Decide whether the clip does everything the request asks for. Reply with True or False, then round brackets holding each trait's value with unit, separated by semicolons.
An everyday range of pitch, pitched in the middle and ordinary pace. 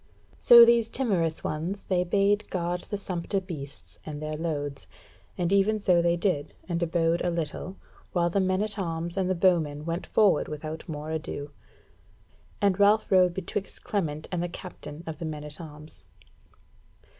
True (3.6 semitones; 175 Hz; 165 wpm)